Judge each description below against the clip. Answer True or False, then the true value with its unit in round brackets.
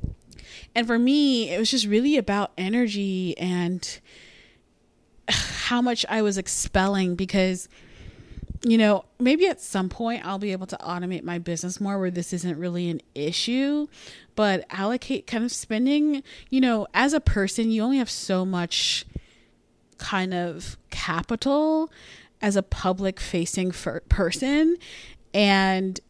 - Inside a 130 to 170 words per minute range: True (140 wpm)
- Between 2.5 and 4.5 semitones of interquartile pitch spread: False (4.9 semitones)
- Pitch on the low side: False (200 Hz)